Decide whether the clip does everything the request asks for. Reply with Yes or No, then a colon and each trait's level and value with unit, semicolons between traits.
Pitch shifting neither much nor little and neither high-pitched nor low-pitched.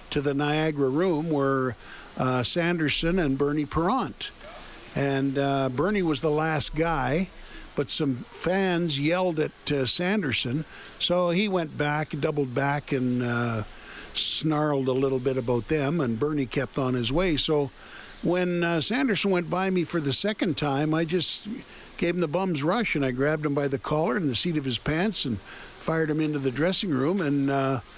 Yes: average, 3.9 semitones; medium, 150 Hz